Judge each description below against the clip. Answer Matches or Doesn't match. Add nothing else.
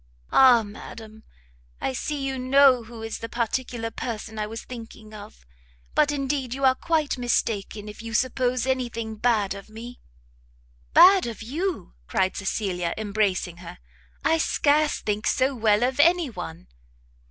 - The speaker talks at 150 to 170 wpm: Matches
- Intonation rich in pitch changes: Doesn't match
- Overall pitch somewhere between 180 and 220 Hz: Doesn't match